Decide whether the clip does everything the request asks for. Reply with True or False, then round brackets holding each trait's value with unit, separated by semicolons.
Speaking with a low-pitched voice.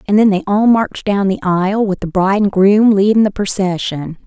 False (200 Hz)